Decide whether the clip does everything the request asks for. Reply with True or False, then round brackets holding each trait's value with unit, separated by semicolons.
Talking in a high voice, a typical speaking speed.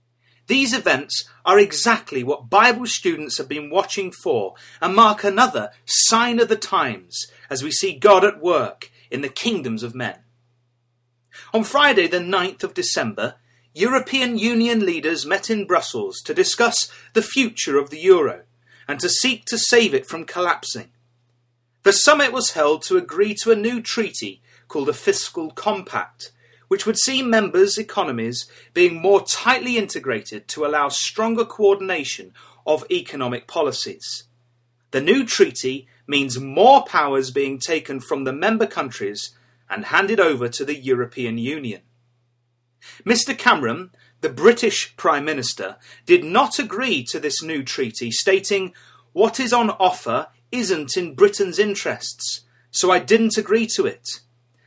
True (195 Hz; 145 wpm)